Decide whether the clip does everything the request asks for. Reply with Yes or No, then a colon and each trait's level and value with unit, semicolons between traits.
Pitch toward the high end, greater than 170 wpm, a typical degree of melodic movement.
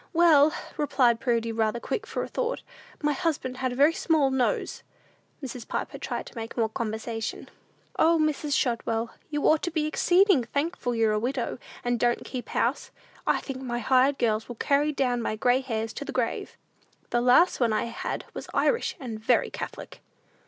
Yes: very high, 255 Hz; average, 180 wpm; average, 4.3 semitones